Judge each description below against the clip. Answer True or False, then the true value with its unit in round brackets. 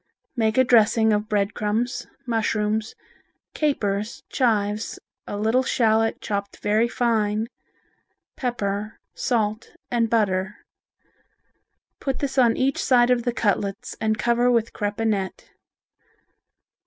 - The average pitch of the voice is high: True (220 Hz)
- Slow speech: True (115 wpm)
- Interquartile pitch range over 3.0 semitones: False (2.5 semitones)